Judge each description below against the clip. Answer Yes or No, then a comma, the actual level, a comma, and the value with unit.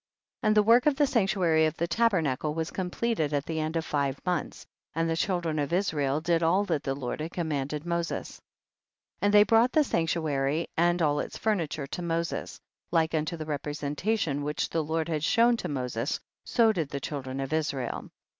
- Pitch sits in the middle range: Yes, medium, 160 Hz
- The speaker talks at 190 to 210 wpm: Yes, average, 200 wpm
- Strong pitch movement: No, average, 3.6 semitones